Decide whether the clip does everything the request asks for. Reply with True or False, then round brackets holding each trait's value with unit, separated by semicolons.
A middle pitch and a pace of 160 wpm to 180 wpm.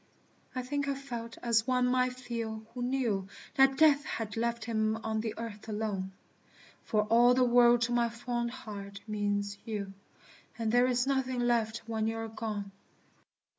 False (230 Hz; 170 wpm)